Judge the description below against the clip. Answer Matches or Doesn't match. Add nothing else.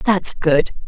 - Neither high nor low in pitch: Matches